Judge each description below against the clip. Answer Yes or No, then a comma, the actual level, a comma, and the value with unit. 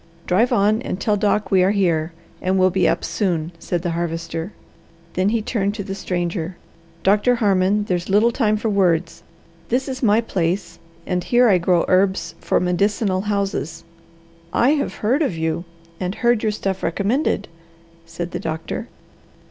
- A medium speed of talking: Yes, average, 165 wpm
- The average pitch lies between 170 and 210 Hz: Yes, high, 190 Hz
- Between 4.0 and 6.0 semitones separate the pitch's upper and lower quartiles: No, average, 3.3 semitones